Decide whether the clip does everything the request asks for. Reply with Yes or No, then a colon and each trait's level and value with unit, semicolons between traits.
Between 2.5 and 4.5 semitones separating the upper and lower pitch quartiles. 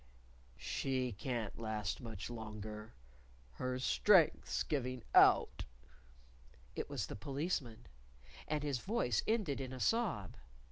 No: average, 4.9 semitones